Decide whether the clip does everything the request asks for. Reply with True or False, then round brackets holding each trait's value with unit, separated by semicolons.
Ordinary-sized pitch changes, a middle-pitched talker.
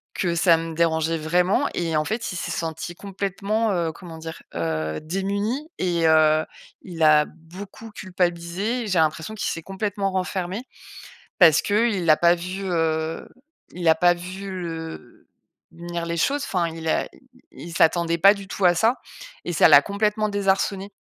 True (3.3 semitones; 175 Hz)